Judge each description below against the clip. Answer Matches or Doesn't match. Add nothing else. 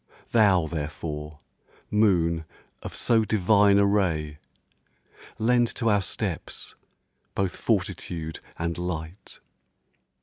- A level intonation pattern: Doesn't match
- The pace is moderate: Doesn't match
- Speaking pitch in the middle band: Doesn't match